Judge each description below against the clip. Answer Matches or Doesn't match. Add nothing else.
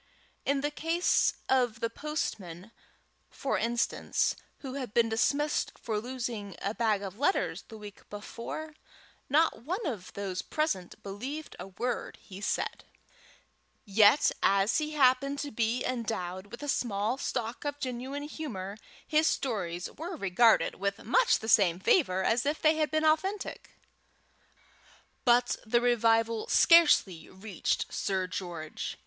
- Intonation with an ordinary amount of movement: Doesn't match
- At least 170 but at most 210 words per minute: Doesn't match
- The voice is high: Matches